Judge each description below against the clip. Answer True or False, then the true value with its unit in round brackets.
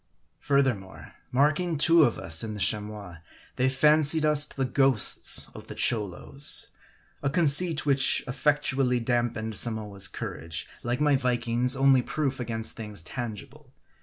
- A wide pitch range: False (4.5 semitones)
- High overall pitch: False (125 Hz)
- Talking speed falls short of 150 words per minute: True (135 wpm)